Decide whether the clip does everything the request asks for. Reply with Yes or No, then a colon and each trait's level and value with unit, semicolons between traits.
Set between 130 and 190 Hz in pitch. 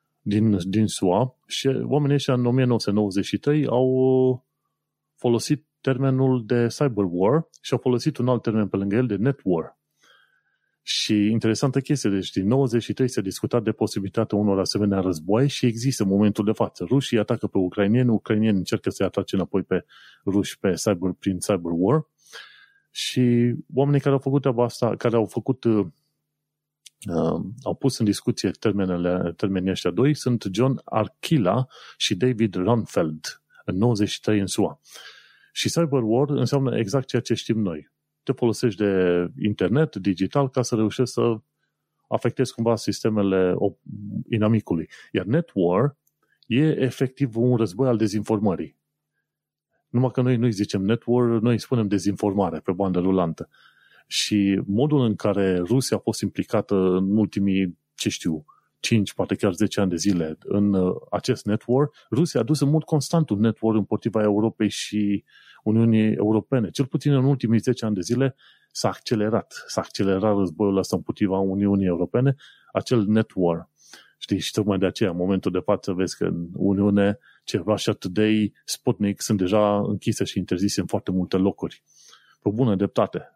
No: low, 110 Hz